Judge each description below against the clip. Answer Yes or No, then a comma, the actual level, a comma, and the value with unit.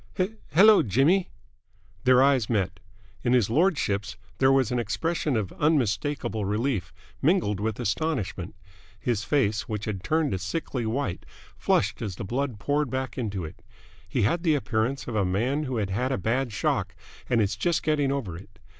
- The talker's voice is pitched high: No, low, 120 Hz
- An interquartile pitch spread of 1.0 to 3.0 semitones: No, wide, 5.5 semitones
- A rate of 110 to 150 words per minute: No, average, 170 wpm